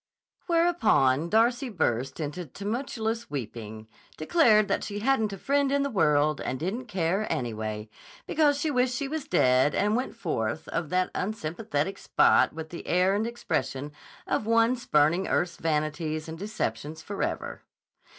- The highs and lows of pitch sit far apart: Yes, wide, 7.6 semitones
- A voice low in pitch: No, medium, 185 Hz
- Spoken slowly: No, average, 150 wpm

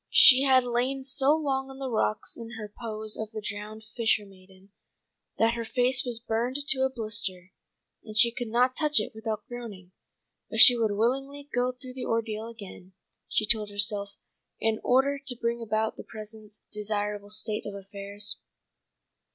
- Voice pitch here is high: Yes, high, 225 Hz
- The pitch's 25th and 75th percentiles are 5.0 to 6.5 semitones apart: No, average, 3.0 semitones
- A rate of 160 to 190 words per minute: Yes, average, 170 wpm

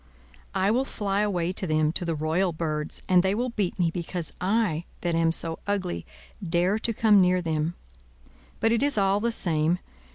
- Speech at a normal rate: Yes, average, 190 wpm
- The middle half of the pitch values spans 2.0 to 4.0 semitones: Yes, average, 3.7 semitones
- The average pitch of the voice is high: No, medium, 180 Hz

